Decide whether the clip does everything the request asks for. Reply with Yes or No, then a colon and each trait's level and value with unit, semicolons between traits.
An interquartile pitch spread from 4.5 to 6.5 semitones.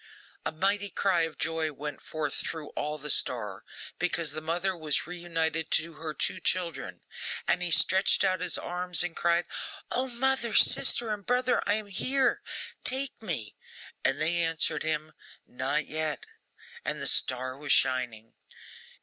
No: average, 3.8 semitones